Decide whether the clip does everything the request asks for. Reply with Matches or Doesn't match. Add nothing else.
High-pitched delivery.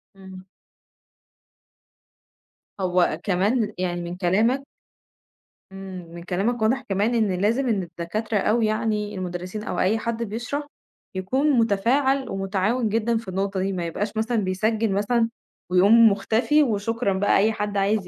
Matches